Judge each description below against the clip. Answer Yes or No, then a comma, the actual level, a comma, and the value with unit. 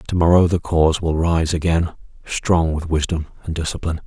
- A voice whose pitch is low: Yes, very low, 80 Hz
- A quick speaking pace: No, average, 175 wpm